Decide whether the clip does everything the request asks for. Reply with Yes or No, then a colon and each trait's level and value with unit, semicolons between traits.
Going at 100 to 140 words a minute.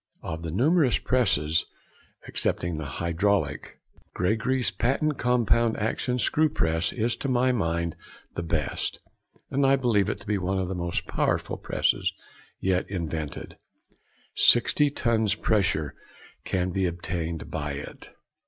Yes: slow, 135 wpm